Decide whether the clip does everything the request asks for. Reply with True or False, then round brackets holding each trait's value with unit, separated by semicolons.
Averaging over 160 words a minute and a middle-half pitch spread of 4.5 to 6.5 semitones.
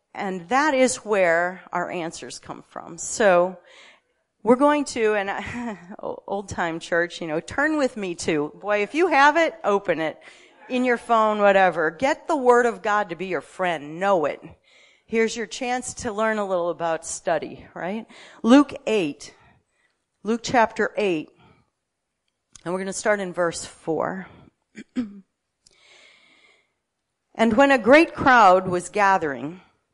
False (150 wpm; 5.4 semitones)